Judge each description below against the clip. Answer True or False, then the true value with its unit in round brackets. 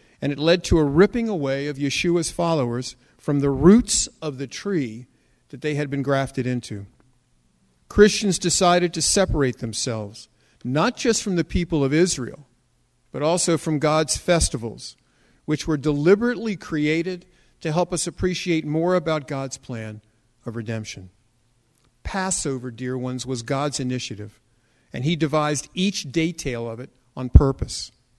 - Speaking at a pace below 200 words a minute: True (145 wpm)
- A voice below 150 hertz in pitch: True (140 Hz)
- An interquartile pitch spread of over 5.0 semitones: True (5.5 semitones)